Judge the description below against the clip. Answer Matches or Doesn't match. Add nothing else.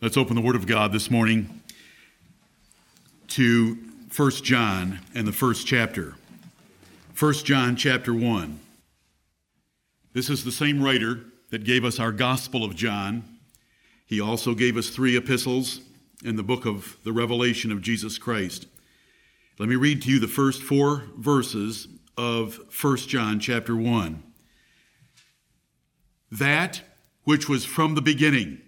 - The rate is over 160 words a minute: Doesn't match